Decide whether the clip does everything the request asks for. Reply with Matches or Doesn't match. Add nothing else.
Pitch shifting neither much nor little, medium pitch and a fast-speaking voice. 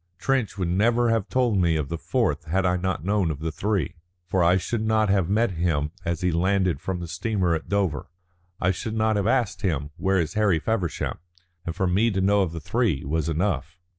Doesn't match